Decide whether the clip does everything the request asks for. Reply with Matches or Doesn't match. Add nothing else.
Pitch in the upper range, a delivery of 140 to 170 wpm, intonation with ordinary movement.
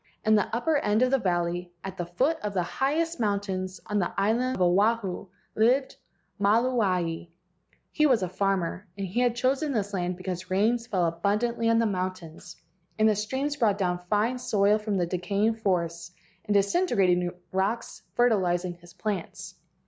Matches